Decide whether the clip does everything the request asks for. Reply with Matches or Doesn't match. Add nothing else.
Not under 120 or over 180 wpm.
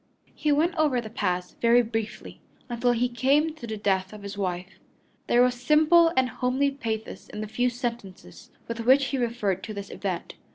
Doesn't match